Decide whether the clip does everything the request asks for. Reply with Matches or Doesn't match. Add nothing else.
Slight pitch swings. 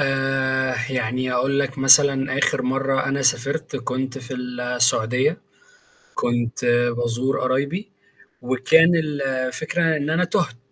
Matches